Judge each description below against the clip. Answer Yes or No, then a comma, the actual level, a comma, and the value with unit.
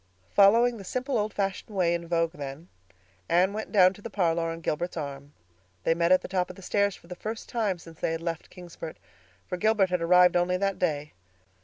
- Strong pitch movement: No, average, 3.1 semitones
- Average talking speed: No, fast, 215 wpm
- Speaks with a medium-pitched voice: Yes, medium, 180 Hz